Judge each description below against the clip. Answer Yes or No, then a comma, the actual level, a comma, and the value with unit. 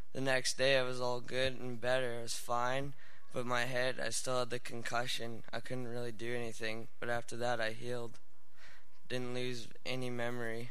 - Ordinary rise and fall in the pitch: No, narrow, 1.2 semitones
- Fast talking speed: No, average, 185 wpm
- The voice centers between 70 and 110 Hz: No, low, 125 Hz